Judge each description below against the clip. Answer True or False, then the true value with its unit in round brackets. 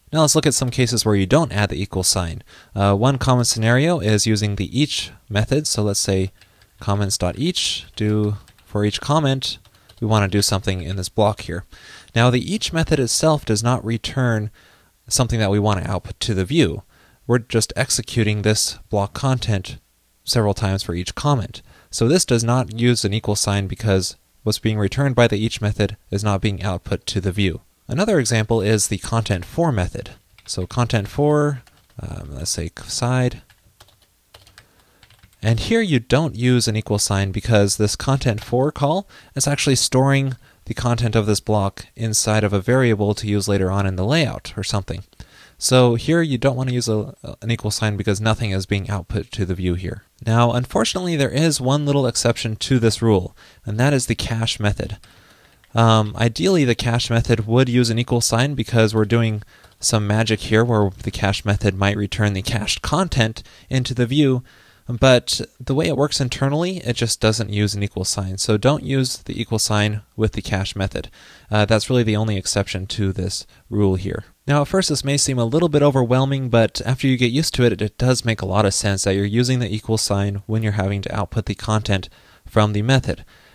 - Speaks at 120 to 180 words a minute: False (195 wpm)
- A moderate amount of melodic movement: True (3.8 semitones)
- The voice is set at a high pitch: False (110 Hz)